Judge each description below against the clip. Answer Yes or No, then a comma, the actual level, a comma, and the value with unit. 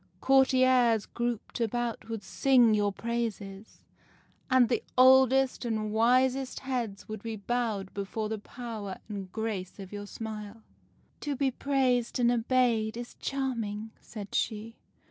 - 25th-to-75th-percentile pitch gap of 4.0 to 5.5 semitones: No, average, 3.1 semitones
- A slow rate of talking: Yes, slow, 130 wpm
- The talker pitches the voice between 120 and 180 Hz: No, high, 230 Hz